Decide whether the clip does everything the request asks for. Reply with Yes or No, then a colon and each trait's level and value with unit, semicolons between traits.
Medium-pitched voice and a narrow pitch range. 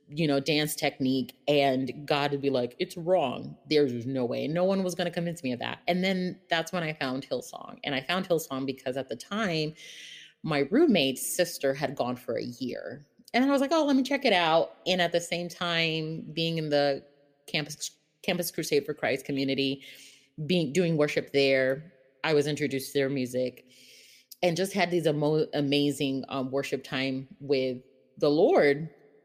No: medium, 145 Hz; average, 4.2 semitones